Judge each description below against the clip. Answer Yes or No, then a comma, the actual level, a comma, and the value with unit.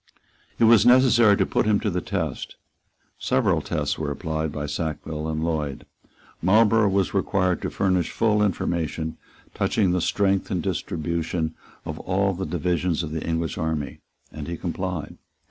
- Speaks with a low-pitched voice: Yes, very low, 85 Hz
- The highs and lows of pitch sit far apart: No, average, 3.7 semitones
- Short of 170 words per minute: Yes, average, 160 wpm